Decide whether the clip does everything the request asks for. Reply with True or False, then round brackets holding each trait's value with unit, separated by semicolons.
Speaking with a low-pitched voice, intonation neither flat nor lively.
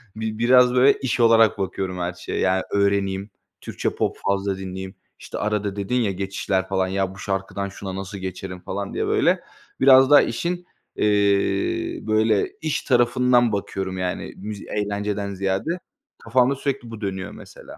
True (100 Hz; 3.7 semitones)